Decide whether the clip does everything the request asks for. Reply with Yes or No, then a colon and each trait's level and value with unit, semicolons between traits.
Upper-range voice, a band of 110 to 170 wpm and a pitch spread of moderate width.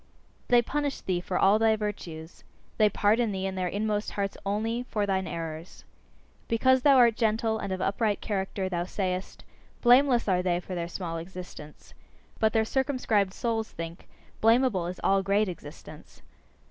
Yes: high, 200 Hz; average, 160 wpm; average, 3.6 semitones